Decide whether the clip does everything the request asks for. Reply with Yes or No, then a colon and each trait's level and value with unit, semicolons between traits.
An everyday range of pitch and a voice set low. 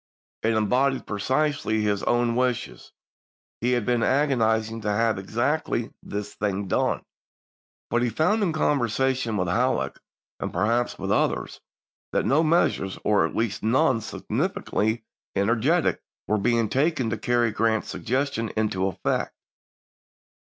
Yes: average, 3.5 semitones; low, 115 Hz